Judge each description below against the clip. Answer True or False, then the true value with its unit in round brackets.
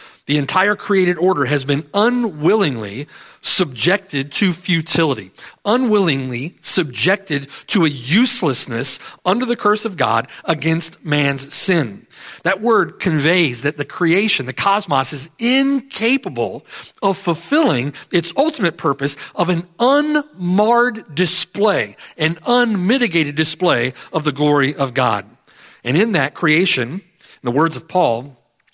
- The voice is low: False (175 Hz)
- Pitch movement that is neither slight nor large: False (6.1 semitones)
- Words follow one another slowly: True (125 wpm)